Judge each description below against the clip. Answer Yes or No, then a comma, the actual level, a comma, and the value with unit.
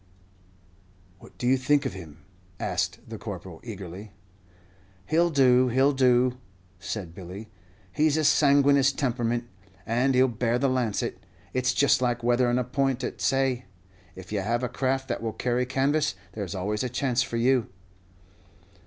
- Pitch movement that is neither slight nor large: Yes, average, 3.1 semitones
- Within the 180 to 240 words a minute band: No, average, 160 wpm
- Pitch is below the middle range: Yes, low, 125 Hz